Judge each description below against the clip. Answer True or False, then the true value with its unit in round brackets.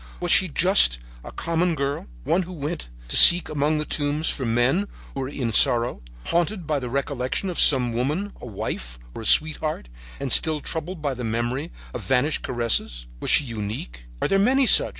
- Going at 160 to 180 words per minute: False (190 wpm)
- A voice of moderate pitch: True (145 Hz)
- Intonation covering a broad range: True (5.7 semitones)